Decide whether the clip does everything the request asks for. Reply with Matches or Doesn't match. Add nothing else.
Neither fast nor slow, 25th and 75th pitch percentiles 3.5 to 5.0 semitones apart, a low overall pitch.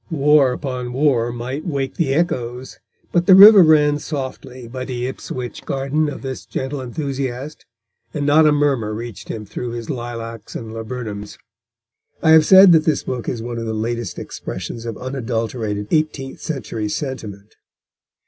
Matches